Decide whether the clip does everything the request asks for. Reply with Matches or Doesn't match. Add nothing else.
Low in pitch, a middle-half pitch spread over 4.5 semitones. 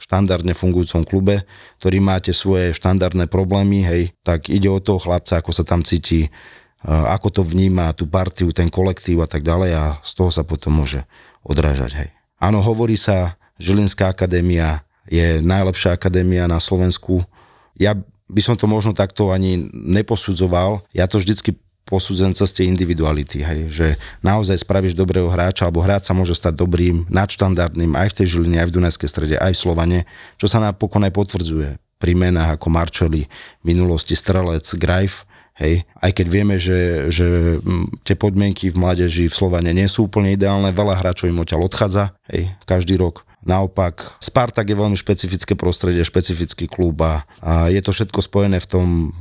Doesn't match